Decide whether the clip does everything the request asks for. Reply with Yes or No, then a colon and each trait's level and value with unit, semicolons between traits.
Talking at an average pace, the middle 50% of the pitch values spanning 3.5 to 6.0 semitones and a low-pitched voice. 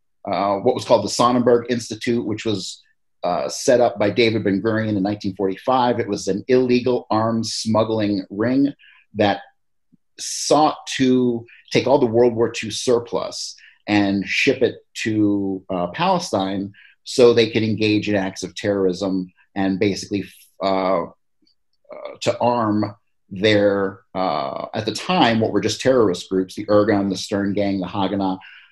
No: average, 150 wpm; average, 3.1 semitones; low, 105 Hz